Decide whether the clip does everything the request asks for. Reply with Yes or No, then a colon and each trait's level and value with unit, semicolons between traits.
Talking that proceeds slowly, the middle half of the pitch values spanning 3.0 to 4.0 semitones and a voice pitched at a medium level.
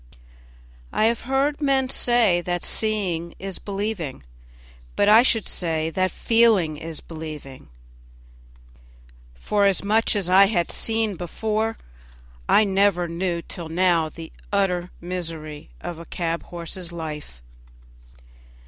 No: slow, 120 wpm; average, 4.4 semitones; medium, 180 Hz